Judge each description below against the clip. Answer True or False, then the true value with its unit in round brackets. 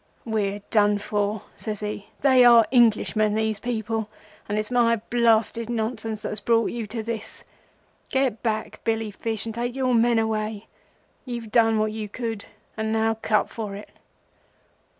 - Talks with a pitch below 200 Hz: False (220 Hz)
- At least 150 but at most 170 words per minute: True (155 wpm)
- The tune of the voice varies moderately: False (1.6 semitones)